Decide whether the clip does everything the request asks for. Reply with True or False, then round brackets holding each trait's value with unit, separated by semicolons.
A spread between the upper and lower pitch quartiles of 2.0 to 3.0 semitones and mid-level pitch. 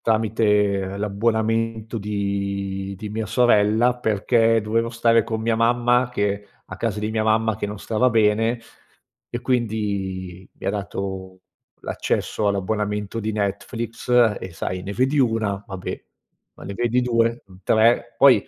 False (2.5 semitones; 110 Hz)